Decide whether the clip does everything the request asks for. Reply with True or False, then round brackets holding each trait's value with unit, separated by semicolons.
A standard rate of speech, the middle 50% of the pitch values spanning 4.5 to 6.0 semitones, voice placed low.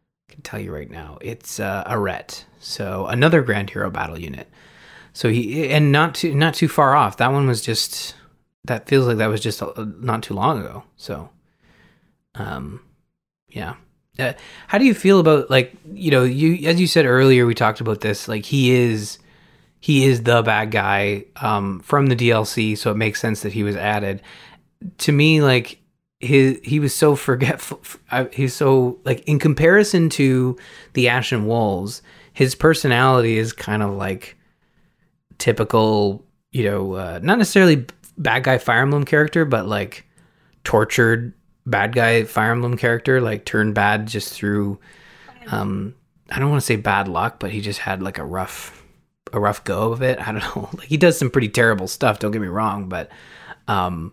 True (180 wpm; 5.1 semitones; 120 Hz)